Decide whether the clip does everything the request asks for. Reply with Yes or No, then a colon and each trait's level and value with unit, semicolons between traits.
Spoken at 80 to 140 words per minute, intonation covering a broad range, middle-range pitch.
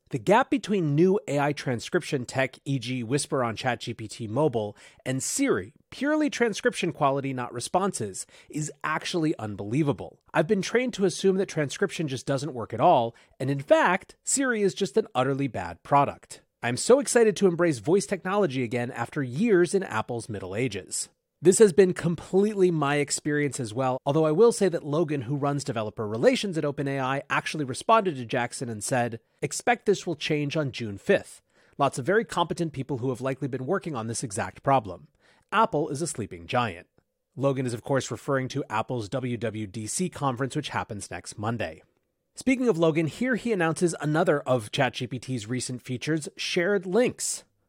No: average, 170 wpm; wide, 6.5 semitones; medium, 145 Hz